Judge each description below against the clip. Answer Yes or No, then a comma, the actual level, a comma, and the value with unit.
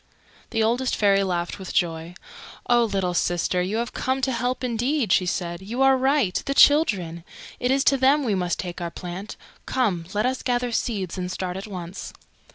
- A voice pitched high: Yes, high, 205 Hz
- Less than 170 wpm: No, average, 190 wpm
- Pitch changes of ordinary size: No, wide, 5.9 semitones